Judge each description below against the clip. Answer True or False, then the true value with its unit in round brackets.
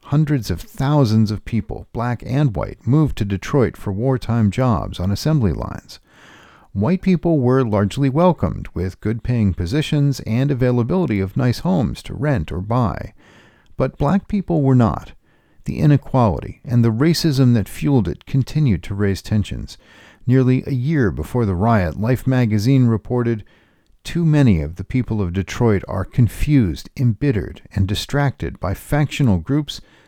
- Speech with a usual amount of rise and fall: False (5.7 semitones)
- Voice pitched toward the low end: True (120 Hz)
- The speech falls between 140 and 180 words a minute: True (150 wpm)